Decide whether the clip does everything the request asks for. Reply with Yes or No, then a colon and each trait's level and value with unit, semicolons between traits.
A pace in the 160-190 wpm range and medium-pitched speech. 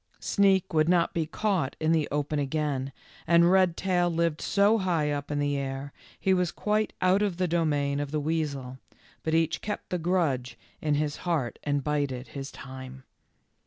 Yes: average, 180 wpm; medium, 155 Hz